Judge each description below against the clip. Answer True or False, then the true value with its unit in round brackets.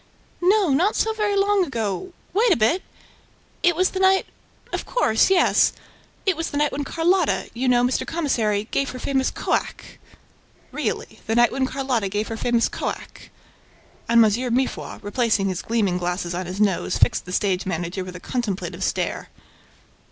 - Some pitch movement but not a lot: False (8.8 semitones)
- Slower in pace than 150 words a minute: False (175 wpm)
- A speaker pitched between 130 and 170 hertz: False (245 Hz)